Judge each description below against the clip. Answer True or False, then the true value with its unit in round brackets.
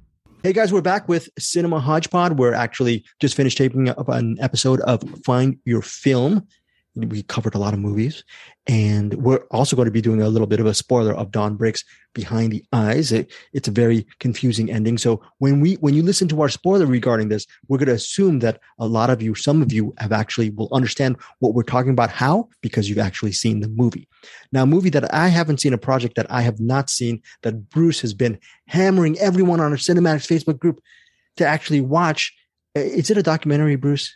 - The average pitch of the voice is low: True (130 Hz)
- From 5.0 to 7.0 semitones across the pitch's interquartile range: True (5.5 semitones)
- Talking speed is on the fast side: True (215 wpm)